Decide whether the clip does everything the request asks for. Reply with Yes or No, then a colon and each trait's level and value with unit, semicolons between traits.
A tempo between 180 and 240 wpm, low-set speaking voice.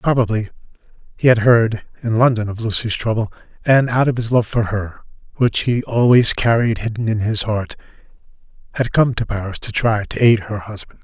Yes: average, 185 wpm; low, 115 Hz